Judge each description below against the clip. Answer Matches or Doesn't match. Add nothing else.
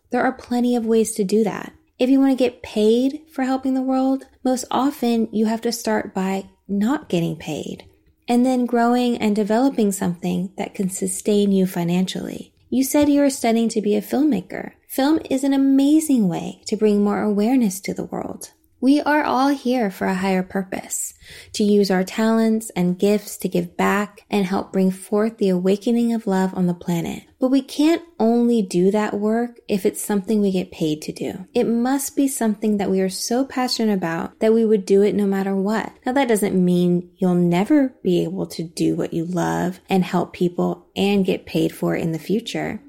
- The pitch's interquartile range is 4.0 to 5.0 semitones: Matches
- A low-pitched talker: Doesn't match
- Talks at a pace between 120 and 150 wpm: Doesn't match